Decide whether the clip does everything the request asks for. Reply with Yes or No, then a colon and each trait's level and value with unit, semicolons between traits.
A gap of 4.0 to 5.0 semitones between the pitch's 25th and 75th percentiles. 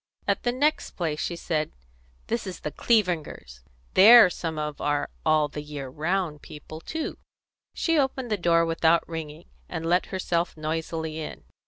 No: average, 3.6 semitones